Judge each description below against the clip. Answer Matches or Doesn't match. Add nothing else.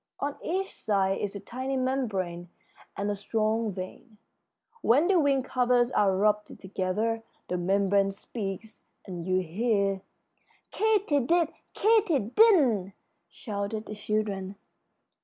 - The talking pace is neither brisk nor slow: Doesn't match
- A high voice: Matches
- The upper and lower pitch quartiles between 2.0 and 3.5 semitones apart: Doesn't match